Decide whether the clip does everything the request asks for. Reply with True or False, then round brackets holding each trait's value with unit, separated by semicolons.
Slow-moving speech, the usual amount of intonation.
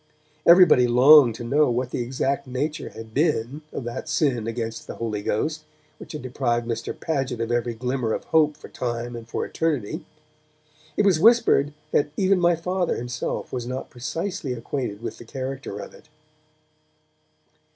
False (165 wpm; 4.4 semitones)